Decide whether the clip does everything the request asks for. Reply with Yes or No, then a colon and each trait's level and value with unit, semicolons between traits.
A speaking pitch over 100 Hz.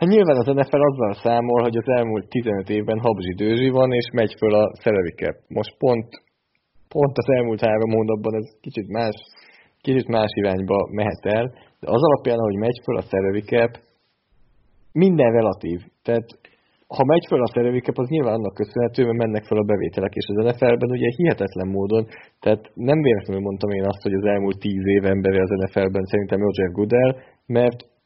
Yes: low, 110 Hz